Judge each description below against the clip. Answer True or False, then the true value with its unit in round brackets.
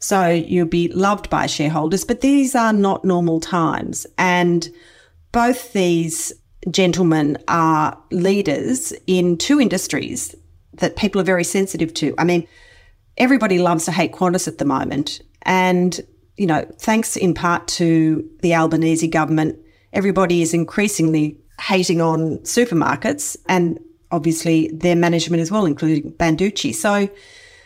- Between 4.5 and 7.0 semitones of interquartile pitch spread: False (3.2 semitones)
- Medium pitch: True (175 Hz)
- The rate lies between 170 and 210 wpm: False (135 wpm)